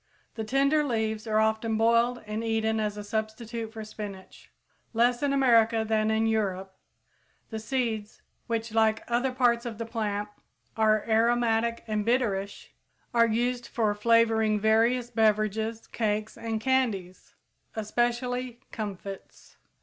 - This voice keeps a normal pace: No, slow, 130 wpm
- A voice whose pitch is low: No, high, 225 Hz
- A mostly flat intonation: Yes, narrow, 1.6 semitones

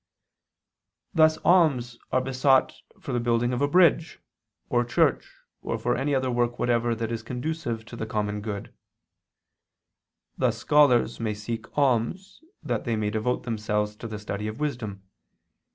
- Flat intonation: No, average, 3.2 semitones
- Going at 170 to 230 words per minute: No, average, 150 wpm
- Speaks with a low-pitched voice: Yes, low, 120 Hz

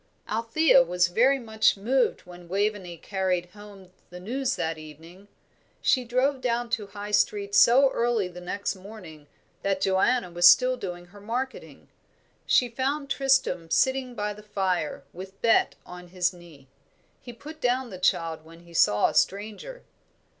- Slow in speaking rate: No, average, 155 wpm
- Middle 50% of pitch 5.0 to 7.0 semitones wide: Yes, wide, 5.6 semitones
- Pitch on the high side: Yes, high, 205 Hz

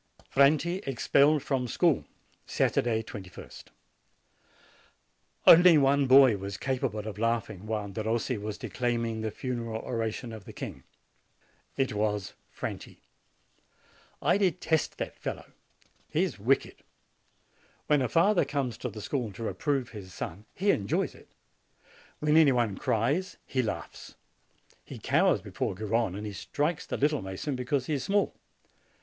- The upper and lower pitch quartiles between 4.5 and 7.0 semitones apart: Yes, average, 4.9 semitones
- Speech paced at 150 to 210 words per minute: No, average, 140 wpm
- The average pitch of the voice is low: Yes, low, 120 Hz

